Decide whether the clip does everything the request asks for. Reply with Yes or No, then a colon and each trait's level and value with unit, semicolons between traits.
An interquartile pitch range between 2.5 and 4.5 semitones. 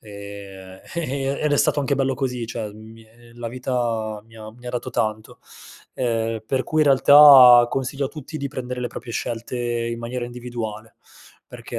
Yes: average, 2.8 semitones